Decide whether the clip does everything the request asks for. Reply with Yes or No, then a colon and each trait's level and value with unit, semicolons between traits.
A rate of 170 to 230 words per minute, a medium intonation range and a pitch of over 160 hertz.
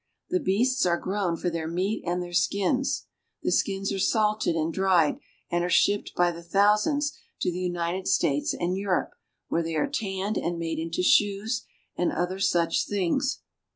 Yes: average, 190 wpm; average, 3.1 semitones; medium, 185 Hz